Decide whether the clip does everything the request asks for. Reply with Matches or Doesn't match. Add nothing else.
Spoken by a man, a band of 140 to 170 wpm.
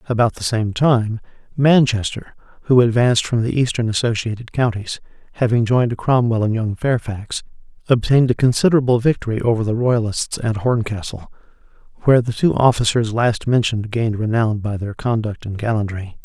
Matches